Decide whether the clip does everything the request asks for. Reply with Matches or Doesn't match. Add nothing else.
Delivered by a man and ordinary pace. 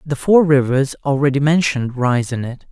Matches